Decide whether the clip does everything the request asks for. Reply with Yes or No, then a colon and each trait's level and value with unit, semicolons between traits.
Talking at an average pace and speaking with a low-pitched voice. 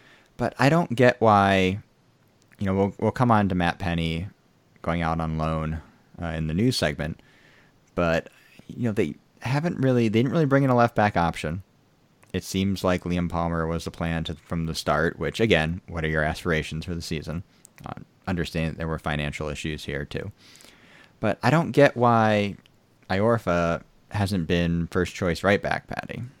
Yes: average, 180 wpm; very low, 90 Hz